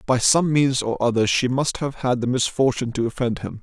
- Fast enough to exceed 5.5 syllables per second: No, 5.4 syllables/s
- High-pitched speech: No, low, 125 Hz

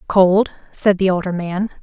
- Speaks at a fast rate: No, average, 165 wpm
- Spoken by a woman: Yes, female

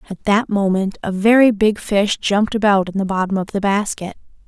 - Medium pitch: No, high, 200 Hz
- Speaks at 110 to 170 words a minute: No, average, 200 wpm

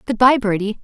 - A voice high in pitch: Yes, high, 225 Hz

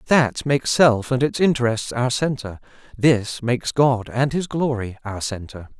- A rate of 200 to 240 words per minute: No, average, 165 wpm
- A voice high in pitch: No, low, 125 Hz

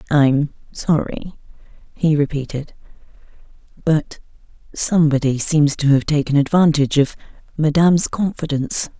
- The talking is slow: Yes, slow, 95 wpm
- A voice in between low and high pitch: Yes, medium, 150 Hz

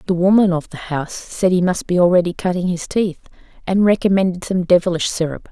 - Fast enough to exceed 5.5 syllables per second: Yes, 6.0 syllables/s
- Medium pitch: Yes, medium, 180 Hz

